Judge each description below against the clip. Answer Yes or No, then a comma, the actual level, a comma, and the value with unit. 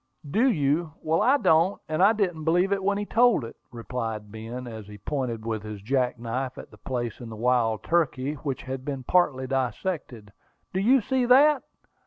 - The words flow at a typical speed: Yes, average, 195 wpm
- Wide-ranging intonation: Yes, wide, 8.0 semitones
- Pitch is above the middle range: No, low, 135 Hz